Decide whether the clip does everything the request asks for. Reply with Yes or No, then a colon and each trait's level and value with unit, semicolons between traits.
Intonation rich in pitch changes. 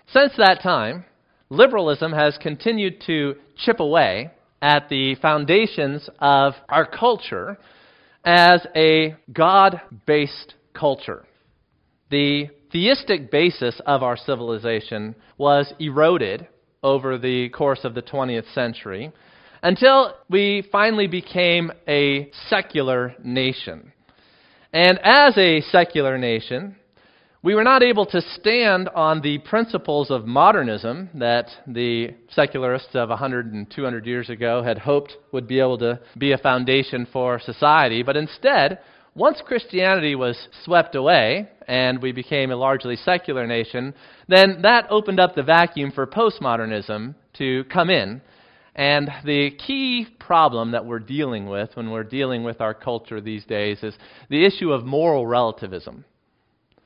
Yes: wide, 6.2 semitones